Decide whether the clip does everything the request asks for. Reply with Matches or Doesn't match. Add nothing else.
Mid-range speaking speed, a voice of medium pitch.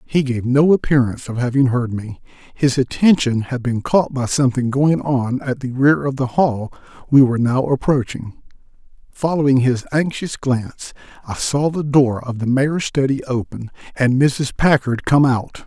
Doesn't match